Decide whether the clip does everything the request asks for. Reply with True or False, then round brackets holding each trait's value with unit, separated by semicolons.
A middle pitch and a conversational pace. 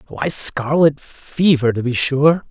True (145 Hz; 145 wpm)